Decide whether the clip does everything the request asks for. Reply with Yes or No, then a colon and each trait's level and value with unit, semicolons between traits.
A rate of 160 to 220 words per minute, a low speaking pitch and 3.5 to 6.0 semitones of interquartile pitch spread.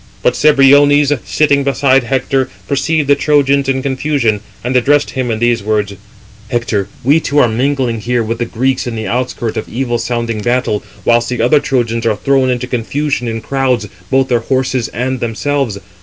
No: average, 175 wpm; low, 125 Hz; average, 2.9 semitones